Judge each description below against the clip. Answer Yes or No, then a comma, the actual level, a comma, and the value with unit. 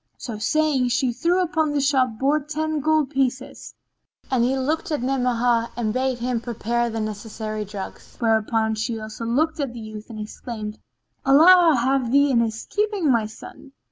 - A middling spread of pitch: Yes, average, 4.4 semitones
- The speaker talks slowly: No, average, 175 wpm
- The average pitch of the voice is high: Yes, very high, 250 Hz